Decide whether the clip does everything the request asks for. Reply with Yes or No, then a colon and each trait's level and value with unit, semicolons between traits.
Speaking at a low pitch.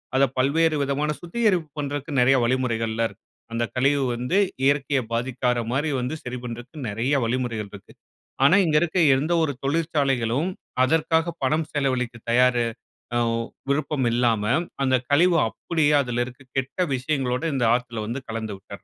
Yes: low, 130 Hz